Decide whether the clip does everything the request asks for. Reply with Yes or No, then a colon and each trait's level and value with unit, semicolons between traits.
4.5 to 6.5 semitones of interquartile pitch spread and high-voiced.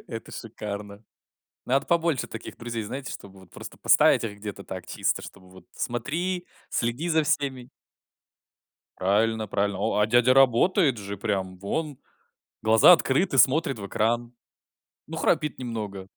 No: average, 5.2 semitones; low, 115 Hz